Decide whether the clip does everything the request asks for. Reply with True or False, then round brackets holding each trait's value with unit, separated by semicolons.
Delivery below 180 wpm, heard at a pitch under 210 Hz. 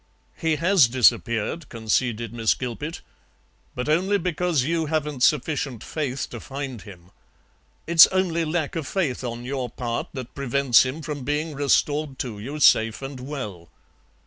True (145 wpm; 140 Hz)